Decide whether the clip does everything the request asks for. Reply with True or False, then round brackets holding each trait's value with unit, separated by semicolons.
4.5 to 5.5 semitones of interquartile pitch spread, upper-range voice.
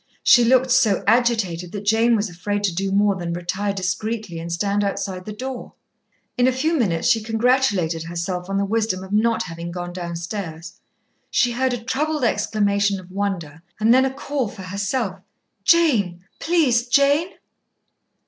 True (4.9 semitones; 205 Hz)